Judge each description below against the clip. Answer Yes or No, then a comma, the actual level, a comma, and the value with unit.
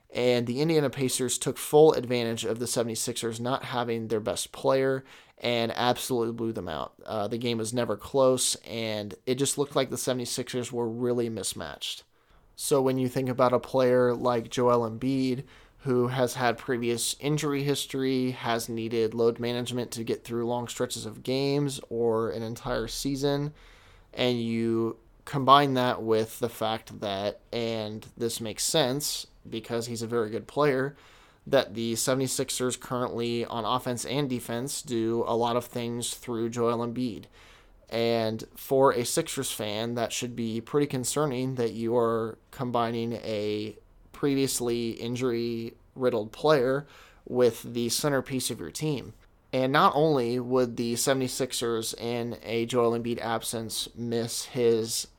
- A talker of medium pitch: No, low, 120 Hz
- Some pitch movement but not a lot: No, narrow, 2.0 semitones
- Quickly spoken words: No, average, 150 wpm